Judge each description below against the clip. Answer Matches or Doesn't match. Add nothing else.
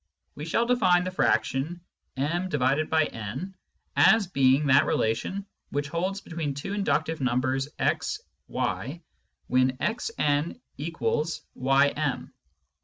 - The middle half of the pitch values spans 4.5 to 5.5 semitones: Matches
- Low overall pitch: Doesn't match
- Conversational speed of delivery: Doesn't match